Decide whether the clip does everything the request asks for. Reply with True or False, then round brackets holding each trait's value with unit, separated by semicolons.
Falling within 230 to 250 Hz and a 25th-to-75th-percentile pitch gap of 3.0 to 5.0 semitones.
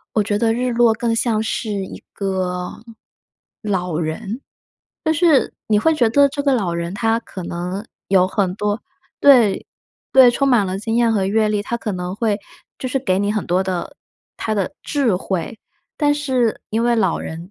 False (215 Hz; 4.1 semitones)